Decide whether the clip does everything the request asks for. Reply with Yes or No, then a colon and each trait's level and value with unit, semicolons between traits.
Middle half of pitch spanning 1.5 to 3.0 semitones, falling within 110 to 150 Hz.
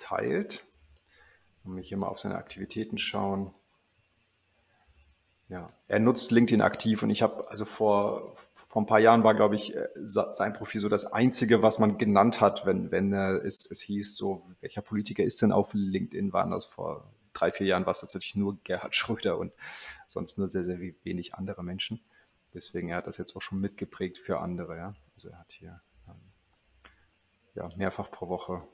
No: average, 2.7 semitones; low, 100 Hz